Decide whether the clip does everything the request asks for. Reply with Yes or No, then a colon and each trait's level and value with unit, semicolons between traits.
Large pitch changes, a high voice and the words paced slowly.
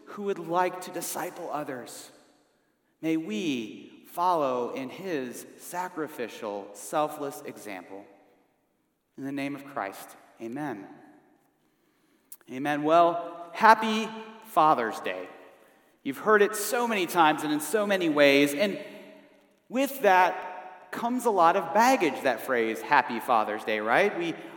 No: wide, 7.2 semitones; medium, 180 Hz; slow, 125 wpm